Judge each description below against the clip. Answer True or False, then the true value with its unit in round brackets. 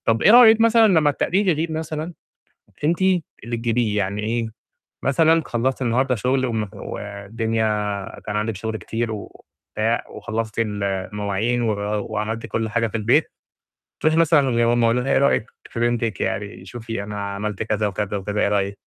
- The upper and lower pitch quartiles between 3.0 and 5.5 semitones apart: True (3.7 semitones)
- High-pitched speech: False (115 Hz)